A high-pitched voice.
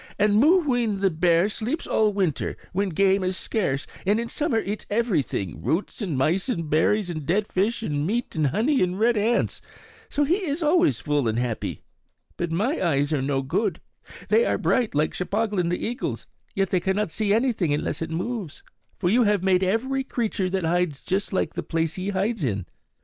Yes: high, 195 Hz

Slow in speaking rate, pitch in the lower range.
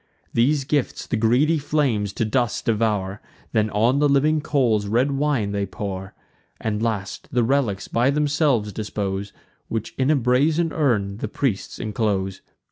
No: average, 150 wpm; low, 115 Hz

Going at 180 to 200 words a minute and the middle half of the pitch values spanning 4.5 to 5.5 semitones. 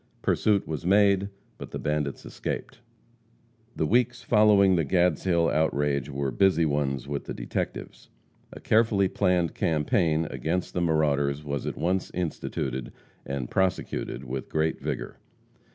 No: slow, 135 wpm; average, 4.9 semitones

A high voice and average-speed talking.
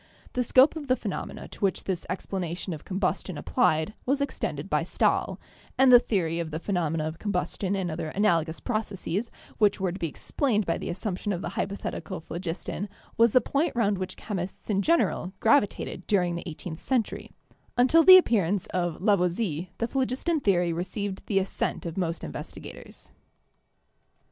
Yes: high, 195 Hz; average, 170 wpm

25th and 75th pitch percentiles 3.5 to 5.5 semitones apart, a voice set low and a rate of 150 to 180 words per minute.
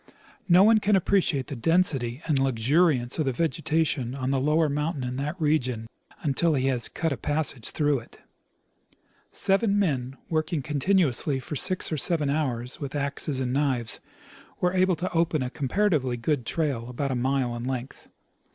No: average, 4.2 semitones; medium, 145 Hz; average, 170 wpm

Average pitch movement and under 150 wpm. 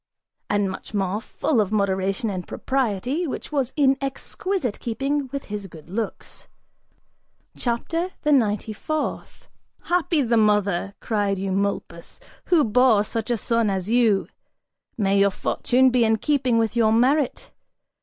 Yes: average, 4.9 semitones; average, 140 wpm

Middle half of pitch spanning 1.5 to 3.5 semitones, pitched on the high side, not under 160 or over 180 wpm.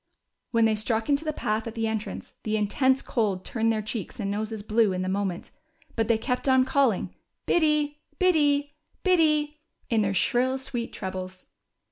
No: average, 4.9 semitones; high, 230 Hz; average, 170 wpm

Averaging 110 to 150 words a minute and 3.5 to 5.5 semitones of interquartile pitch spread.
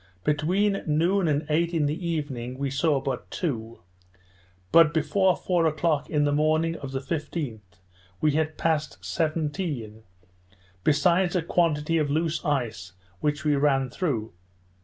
No: average, 140 wpm; average, 3.1 semitones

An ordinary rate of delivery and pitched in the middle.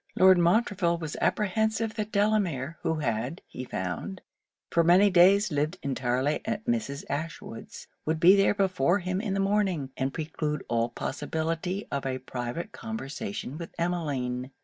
Yes: average, 150 wpm; medium, 170 Hz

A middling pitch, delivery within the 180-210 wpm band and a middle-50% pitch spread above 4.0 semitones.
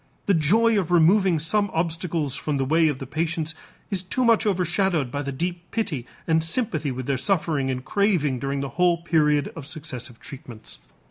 Yes: medium, 160 Hz; average, 185 wpm; average, 4.4 semitones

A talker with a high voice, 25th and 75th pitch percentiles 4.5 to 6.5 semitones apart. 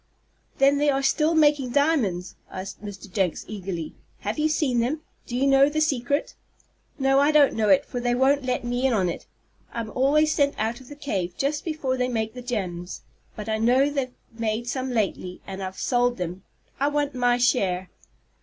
Yes: very high, 250 Hz; average, 4.9 semitones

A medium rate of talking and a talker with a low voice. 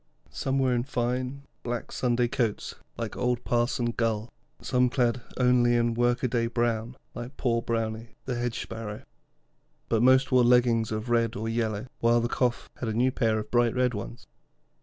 Yes: average, 180 wpm; low, 120 Hz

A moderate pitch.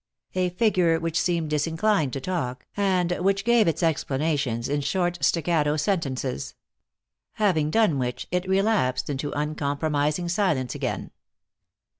Yes: medium, 165 Hz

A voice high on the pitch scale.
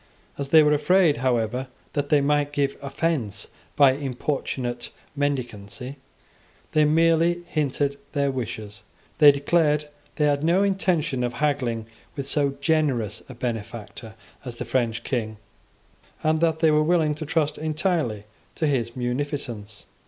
No: medium, 140 Hz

